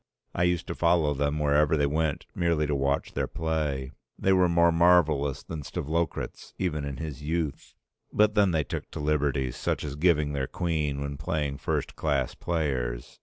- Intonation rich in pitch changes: No, average, 3.0 semitones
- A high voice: No, very low, 75 Hz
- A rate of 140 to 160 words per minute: No, average, 175 wpm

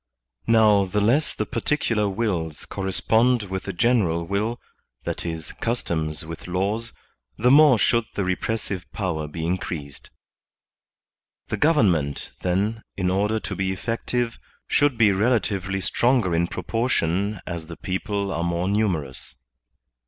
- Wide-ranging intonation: No, average, 4.7 semitones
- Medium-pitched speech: No, low, 100 Hz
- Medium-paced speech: No, slow, 130 wpm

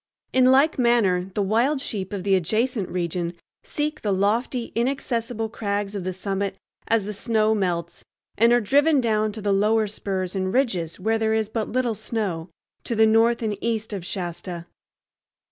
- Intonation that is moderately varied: Yes, average, 3.3 semitones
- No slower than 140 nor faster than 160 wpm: No, average, 175 wpm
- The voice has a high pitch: Yes, high, 215 Hz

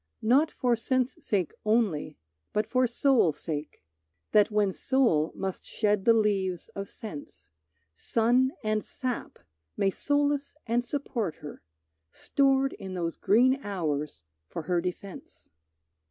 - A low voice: No, high, 215 Hz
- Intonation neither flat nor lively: No, wide, 5.8 semitones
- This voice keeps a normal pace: No, slow, 125 wpm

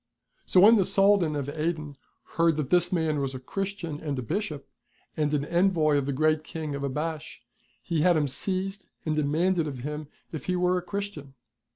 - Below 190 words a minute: No, average, 195 wpm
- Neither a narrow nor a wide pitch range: Yes, average, 3.7 semitones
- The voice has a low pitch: No, medium, 155 Hz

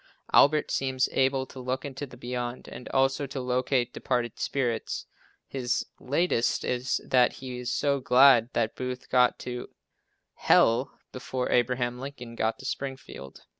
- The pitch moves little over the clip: Yes, narrow, 1.5 semitones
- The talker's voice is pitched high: No, low, 125 Hz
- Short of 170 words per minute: Yes, average, 150 wpm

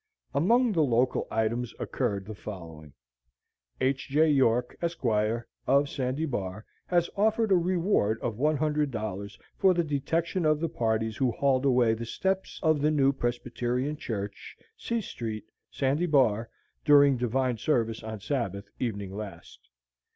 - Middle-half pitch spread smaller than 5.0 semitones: No, wide, 5.6 semitones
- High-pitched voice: No, low, 130 Hz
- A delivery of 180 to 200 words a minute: No, average, 140 wpm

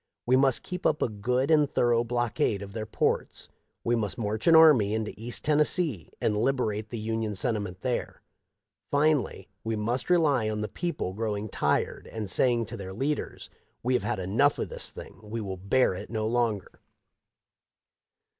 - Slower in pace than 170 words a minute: No, average, 175 wpm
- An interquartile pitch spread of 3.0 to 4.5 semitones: Yes, average, 3.7 semitones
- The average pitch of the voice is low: Yes, low, 115 Hz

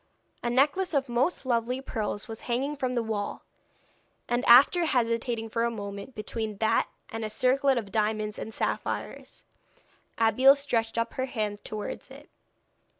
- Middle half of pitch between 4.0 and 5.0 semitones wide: No, average, 3.2 semitones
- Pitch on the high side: Yes, high, 235 Hz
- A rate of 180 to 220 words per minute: No, average, 150 wpm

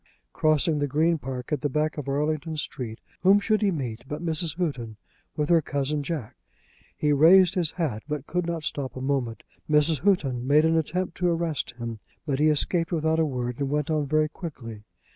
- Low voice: No, medium, 150 Hz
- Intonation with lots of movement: No, average, 3.4 semitones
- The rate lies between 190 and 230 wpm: Yes, average, 200 wpm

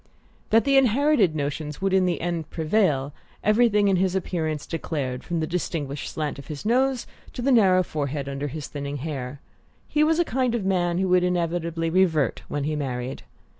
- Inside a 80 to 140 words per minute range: No, average, 185 wpm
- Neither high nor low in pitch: Yes, medium, 170 Hz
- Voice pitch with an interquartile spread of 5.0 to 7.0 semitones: Yes, average, 5.3 semitones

